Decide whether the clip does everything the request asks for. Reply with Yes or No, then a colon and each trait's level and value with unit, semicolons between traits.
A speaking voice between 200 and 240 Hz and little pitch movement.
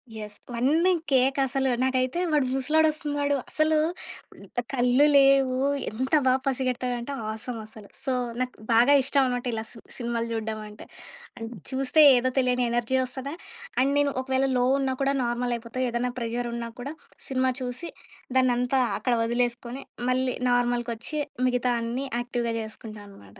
No: very high, 250 Hz; narrow, 2.1 semitones